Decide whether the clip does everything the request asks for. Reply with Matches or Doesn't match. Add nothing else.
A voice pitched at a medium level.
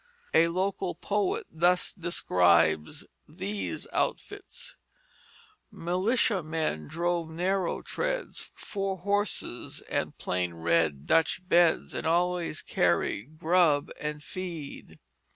Matches